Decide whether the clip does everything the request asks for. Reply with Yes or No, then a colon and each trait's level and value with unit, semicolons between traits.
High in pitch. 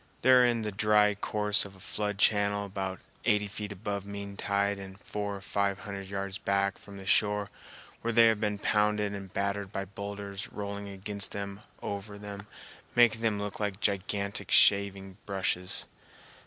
No: low, 100 Hz